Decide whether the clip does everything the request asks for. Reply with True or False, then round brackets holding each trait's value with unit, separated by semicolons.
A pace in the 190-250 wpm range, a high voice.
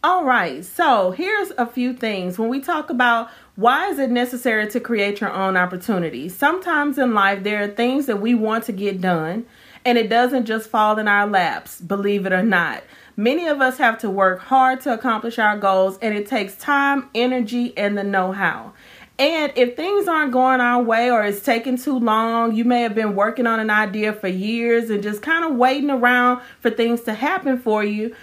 True (205 wpm; 235 Hz)